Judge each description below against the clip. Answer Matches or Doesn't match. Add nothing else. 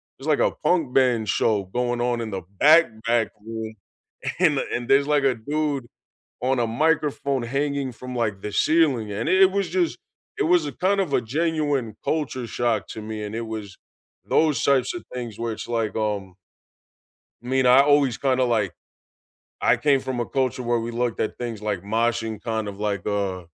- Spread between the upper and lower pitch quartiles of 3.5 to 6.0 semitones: Matches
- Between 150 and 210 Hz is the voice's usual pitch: Doesn't match